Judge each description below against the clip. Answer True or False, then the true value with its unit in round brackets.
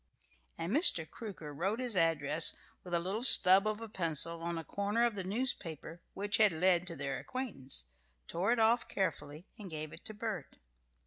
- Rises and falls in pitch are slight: False (4.7 semitones)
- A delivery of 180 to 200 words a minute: True (185 wpm)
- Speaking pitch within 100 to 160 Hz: False (185 Hz)